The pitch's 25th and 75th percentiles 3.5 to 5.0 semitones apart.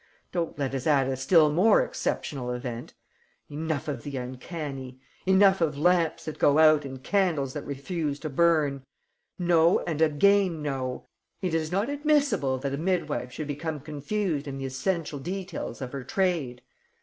Yes: average, 4.4 semitones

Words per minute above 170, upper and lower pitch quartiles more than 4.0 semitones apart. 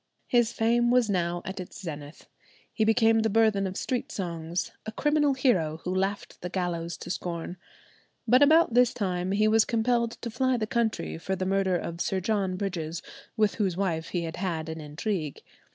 Yes: average, 185 wpm; average, 4.6 semitones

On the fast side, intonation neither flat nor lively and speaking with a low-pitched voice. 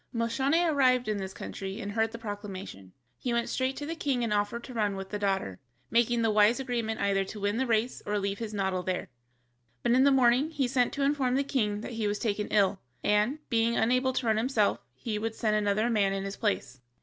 No: fast, 230 wpm; average, 3.5 semitones; high, 225 Hz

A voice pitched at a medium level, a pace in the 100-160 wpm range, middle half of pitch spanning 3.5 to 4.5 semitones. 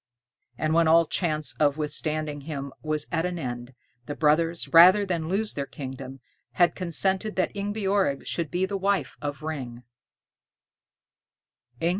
Yes: medium, 160 Hz; average, 140 wpm; average, 4.1 semitones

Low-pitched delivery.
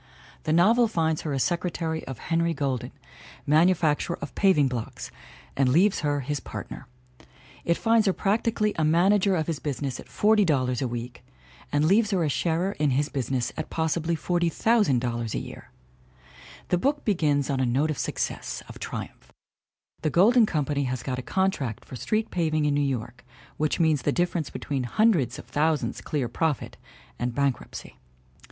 No: medium, 155 Hz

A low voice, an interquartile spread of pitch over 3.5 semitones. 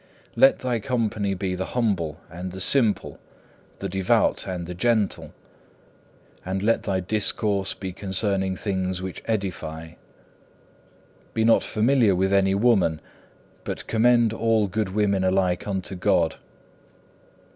No: low, 100 Hz; average, 2.9 semitones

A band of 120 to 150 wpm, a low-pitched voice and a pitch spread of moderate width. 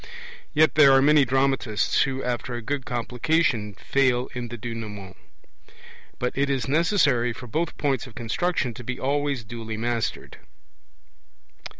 Yes: average, 140 wpm; low, 125 Hz; average, 3.0 semitones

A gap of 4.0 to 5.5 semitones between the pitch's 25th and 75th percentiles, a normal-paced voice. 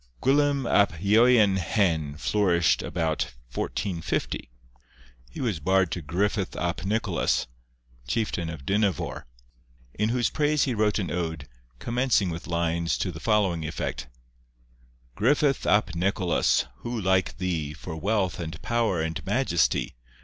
No: average, 4.6 semitones; slow, 130 wpm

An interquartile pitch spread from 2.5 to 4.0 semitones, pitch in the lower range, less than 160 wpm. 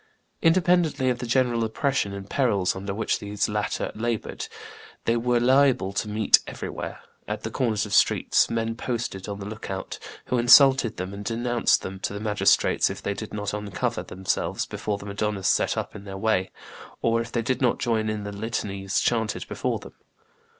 No: average, 3.1 semitones; low, 110 Hz; average, 185 wpm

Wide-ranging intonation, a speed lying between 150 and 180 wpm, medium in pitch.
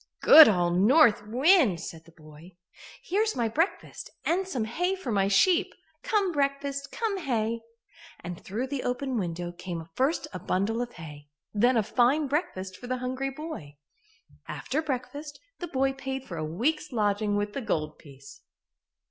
No: wide, 7.4 semitones; average, 165 wpm; high, 245 Hz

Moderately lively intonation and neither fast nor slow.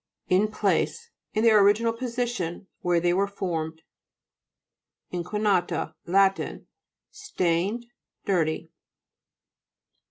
No: average, 4.6 semitones; slow, 85 wpm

